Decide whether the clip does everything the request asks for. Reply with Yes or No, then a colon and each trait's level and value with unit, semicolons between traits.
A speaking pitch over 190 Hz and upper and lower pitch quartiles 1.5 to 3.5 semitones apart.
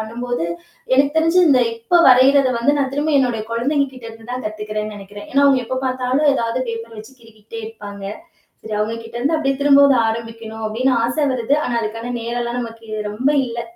Yes: high, 235 Hz; average, 2.9 semitones